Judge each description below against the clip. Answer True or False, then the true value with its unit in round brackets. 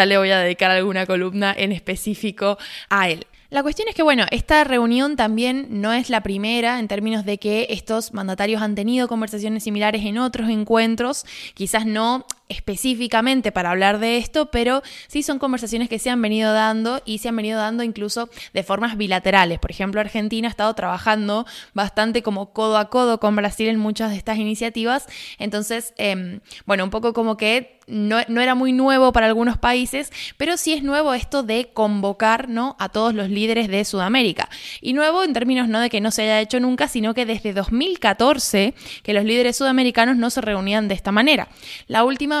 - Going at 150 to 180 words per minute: False (190 wpm)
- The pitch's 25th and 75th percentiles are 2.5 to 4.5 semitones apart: True (2.9 semitones)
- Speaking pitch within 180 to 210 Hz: False (225 Hz)